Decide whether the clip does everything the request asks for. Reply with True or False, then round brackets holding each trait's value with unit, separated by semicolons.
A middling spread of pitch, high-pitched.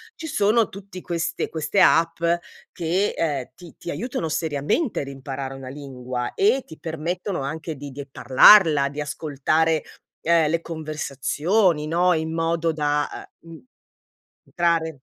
False (3.2 semitones; 160 Hz)